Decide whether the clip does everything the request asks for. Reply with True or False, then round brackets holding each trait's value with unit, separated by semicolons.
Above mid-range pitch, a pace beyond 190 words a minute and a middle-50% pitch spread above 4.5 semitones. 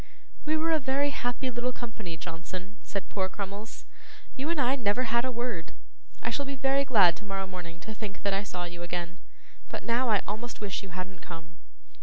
True (210 Hz; 200 wpm; 5.4 semitones)